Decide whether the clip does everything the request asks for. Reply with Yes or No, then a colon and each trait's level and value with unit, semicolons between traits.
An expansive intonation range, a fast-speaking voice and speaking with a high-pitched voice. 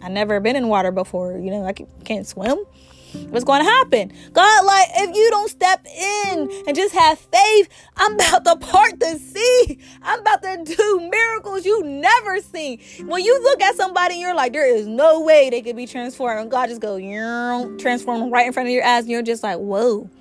Yes: wide, 8.8 semitones; fast, 215 wpm; very high, 320 Hz